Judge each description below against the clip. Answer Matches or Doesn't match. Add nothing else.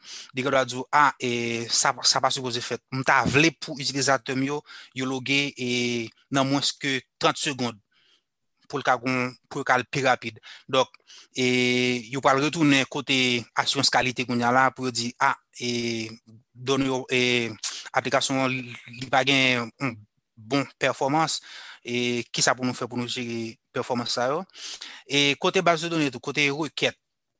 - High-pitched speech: Doesn't match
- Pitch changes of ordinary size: Doesn't match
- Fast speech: Doesn't match